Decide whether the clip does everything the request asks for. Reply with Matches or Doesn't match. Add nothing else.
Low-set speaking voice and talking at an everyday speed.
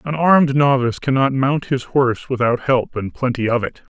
Matches